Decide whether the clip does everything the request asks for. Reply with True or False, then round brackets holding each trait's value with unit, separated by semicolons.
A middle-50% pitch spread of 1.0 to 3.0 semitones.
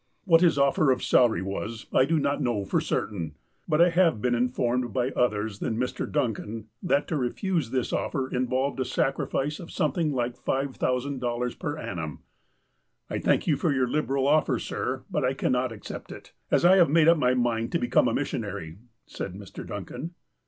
False (3.7 semitones)